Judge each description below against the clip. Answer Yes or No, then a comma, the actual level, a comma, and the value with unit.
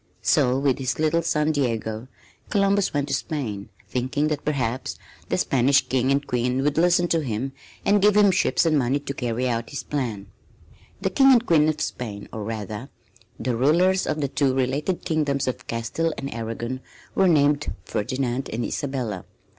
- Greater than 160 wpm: Yes, average, 175 wpm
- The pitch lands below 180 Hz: Yes, low, 135 Hz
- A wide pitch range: No, average, 4.3 semitones